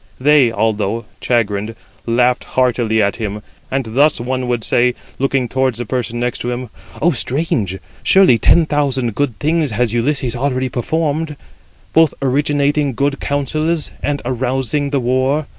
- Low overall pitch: Yes, low, 130 Hz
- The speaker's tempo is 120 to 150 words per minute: Yes, average, 140 wpm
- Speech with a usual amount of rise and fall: Yes, average, 3.3 semitones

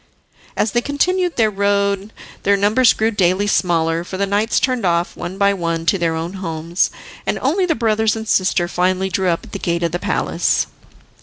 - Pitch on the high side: Yes, high, 195 Hz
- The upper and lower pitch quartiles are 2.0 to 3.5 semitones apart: No, average, 4.0 semitones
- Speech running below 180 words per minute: No, average, 200 wpm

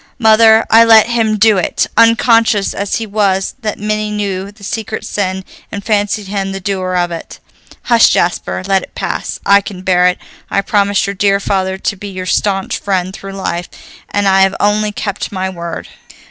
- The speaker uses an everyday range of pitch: No, narrow, 2.0 semitones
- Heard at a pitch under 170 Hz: No, high, 200 Hz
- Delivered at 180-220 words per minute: Yes, average, 190 wpm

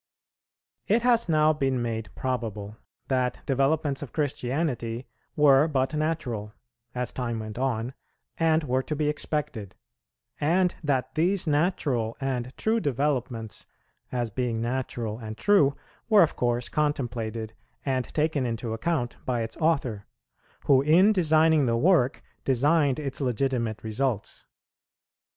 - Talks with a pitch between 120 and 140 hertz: Yes, low, 135 Hz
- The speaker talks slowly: Yes, slow, 130 wpm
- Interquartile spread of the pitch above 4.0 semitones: Yes, average, 4.5 semitones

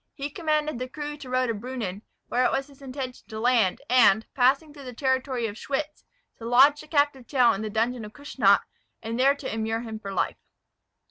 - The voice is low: No, very high, 255 Hz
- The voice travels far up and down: No, average, 3.8 semitones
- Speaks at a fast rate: Yes, fast, 210 wpm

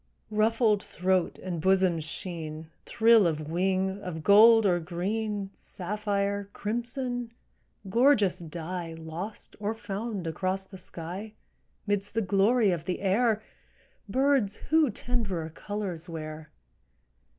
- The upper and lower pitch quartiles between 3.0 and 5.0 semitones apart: Yes, average, 3.8 semitones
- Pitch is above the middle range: Yes, high, 195 Hz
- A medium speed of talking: No, slow, 110 wpm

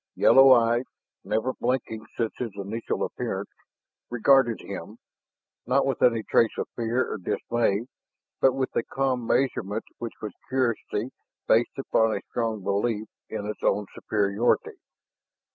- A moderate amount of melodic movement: Yes, average, 3.0 semitones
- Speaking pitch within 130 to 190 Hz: No, low, 115 Hz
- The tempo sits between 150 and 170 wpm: No, slow, 135 wpm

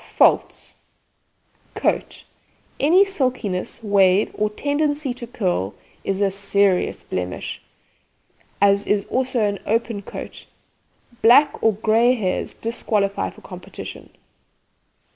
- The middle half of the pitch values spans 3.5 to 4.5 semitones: Yes, average, 3.9 semitones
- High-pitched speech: Yes, high, 210 Hz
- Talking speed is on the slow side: Yes, slow, 105 wpm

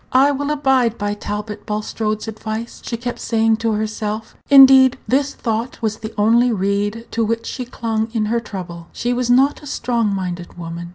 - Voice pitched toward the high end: Yes, high, 225 Hz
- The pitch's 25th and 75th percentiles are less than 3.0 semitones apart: Yes, narrow, 2.6 semitones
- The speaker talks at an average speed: Yes, average, 180 wpm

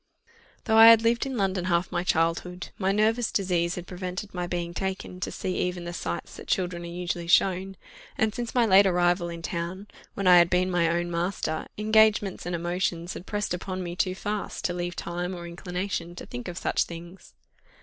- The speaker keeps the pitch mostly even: Yes, narrow, 2.0 semitones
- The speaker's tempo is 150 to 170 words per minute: No, average, 200 wpm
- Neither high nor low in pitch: Yes, medium, 180 Hz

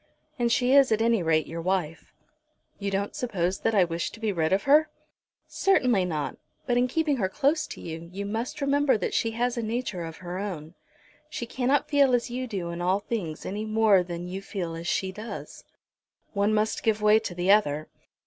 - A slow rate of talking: No, fast, 205 wpm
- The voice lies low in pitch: No, high, 205 Hz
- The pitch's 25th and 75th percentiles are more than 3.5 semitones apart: Yes, average, 5.3 semitones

